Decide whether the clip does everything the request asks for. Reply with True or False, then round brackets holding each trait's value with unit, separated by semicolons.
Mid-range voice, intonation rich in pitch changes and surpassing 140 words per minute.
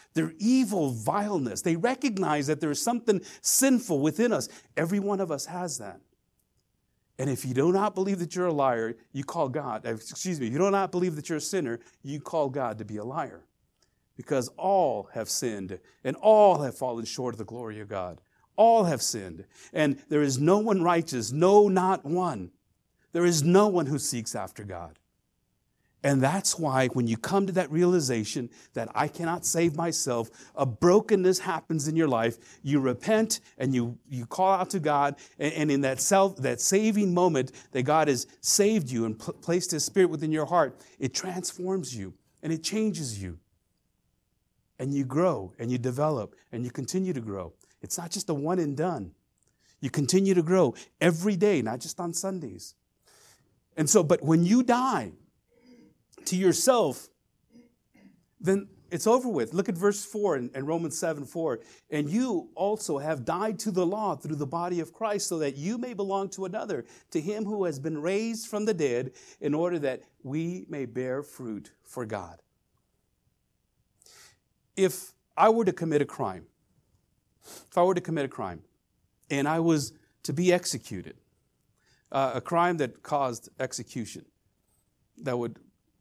True (160 Hz; 6.4 semitones; 175 wpm)